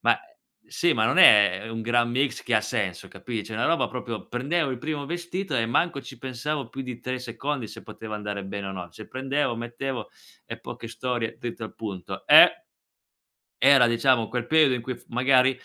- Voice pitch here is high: No, low, 120 Hz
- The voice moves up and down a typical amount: Yes, average, 3.2 semitones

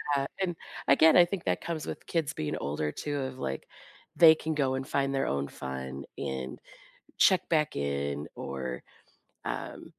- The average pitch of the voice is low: Yes, low, 130 Hz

